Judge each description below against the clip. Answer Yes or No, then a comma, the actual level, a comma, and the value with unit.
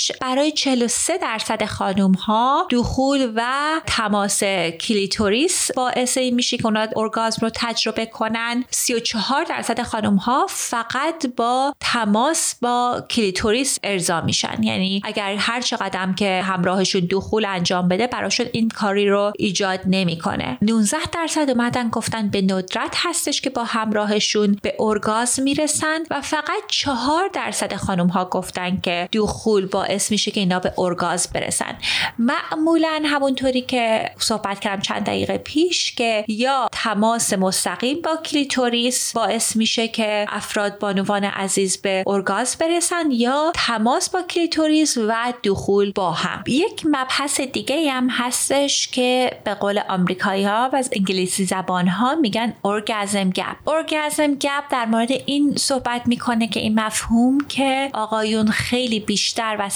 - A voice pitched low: No, high, 230 Hz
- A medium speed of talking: Yes, average, 140 wpm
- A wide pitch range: No, average, 5.0 semitones